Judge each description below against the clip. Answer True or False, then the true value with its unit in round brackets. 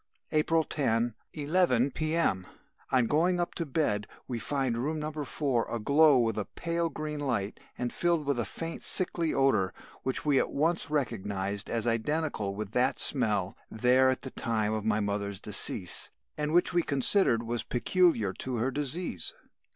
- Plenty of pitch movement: True (5.9 semitones)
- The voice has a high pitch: False (130 Hz)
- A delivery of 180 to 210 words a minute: False (165 wpm)